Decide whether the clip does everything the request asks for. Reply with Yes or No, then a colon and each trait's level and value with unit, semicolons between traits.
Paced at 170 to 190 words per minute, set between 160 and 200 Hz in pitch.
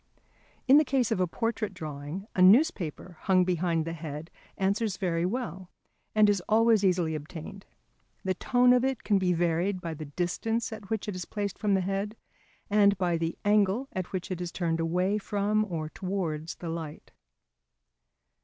Yes: average, 175 wpm; medium, 185 Hz